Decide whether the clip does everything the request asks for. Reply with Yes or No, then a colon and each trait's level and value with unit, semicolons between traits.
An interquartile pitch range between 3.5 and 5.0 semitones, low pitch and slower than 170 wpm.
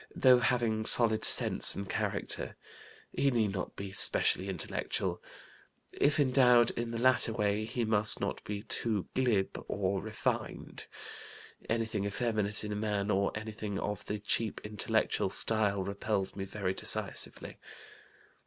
No: narrow, 2.5 semitones; low, 105 Hz; slow, 135 wpm